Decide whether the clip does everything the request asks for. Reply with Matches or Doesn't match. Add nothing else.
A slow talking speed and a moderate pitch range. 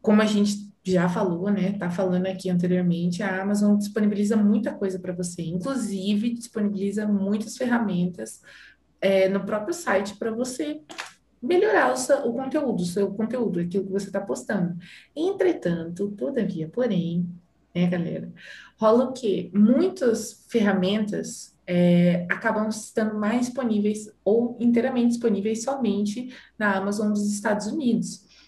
Doesn't match